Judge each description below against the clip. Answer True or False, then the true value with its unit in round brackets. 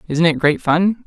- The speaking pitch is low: False (170 Hz)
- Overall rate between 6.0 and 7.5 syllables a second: False (4.5 syllables/s)